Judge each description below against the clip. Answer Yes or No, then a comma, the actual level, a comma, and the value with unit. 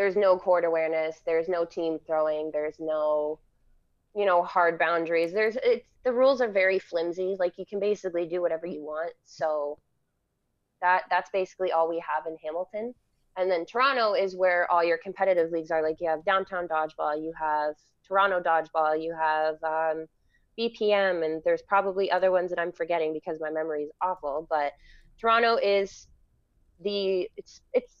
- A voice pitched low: No, medium, 170 Hz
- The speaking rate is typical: Yes, average, 170 wpm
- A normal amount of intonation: Yes, average, 3.3 semitones